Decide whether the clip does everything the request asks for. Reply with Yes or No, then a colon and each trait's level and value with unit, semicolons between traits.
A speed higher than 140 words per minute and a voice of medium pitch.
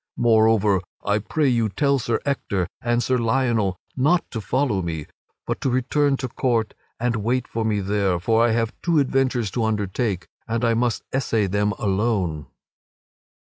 No: average, 170 wpm; low, 115 Hz